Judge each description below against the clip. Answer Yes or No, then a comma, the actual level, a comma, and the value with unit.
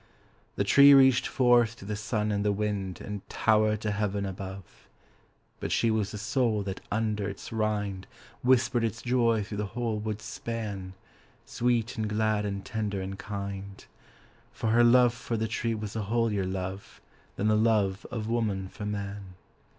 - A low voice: Yes, low, 105 Hz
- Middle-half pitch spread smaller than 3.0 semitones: Yes, narrow, 2.5 semitones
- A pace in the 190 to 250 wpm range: No, average, 170 wpm